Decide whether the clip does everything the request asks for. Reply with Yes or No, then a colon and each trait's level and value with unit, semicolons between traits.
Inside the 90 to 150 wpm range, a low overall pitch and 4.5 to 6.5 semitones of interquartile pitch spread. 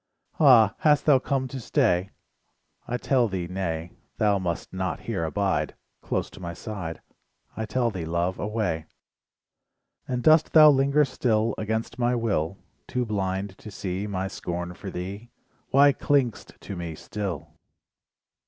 Yes: average, 145 wpm; low, 105 Hz; average, 5.2 semitones